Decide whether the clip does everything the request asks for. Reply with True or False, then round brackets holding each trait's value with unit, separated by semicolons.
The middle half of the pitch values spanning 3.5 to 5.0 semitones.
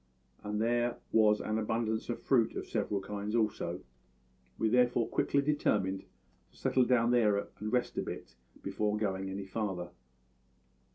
False (2.9 semitones)